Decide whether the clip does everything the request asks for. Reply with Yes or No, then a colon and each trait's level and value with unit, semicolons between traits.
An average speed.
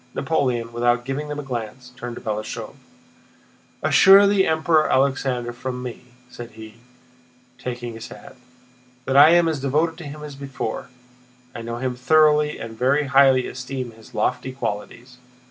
Yes: average, 155 wpm